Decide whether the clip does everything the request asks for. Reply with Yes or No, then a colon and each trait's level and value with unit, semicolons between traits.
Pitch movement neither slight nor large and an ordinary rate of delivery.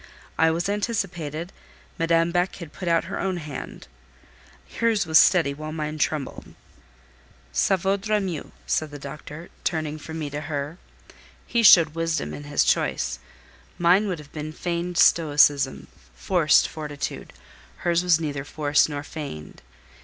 Yes: average, 3.0 semitones; average, 145 wpm